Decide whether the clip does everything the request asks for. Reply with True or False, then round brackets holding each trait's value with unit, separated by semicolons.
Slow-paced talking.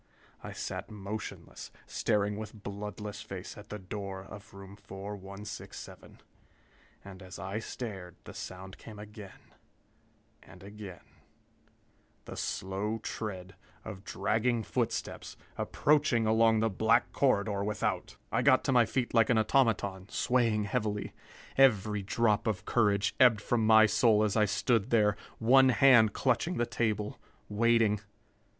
True (130 wpm)